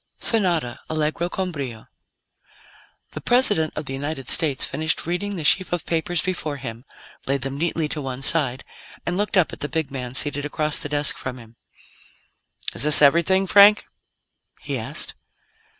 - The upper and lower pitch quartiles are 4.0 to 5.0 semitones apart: Yes, average, 4.4 semitones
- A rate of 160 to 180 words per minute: Yes, average, 165 wpm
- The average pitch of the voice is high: No, medium, 155 Hz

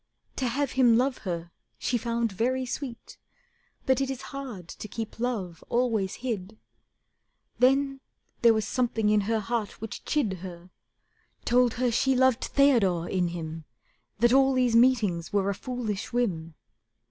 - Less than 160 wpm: Yes, average, 150 wpm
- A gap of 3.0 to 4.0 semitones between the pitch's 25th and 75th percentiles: No, average, 4.7 semitones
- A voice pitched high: Yes, high, 230 Hz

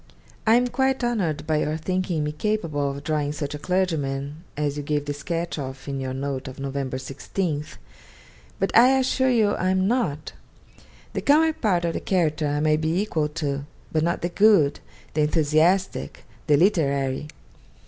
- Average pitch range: Yes, average, 4.6 semitones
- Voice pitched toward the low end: No, medium, 155 Hz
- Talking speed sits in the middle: Yes, average, 175 wpm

